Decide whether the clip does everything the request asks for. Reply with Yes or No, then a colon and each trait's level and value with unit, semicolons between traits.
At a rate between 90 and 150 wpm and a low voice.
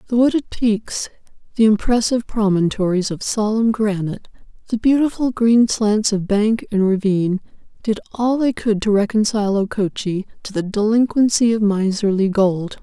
No: average, 140 wpm; high, 210 Hz